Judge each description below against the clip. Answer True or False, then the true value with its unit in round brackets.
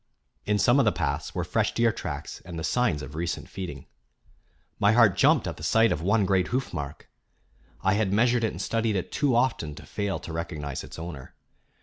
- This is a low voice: True (95 Hz)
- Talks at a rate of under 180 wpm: False (200 wpm)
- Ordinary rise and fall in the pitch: False (5.9 semitones)